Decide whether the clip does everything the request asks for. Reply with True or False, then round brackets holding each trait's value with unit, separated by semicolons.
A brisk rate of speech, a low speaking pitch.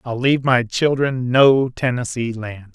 False (155 wpm; 125 Hz)